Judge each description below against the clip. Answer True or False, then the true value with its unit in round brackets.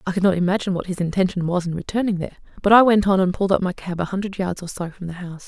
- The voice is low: False (185 Hz)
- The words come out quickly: True (305 wpm)